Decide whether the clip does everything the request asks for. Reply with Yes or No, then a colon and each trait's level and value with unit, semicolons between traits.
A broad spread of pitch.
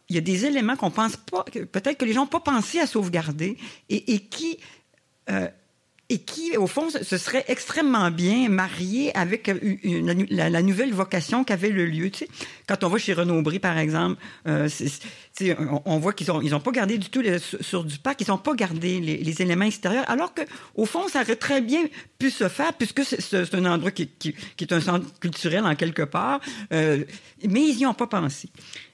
Yes: wide, 6.5 semitones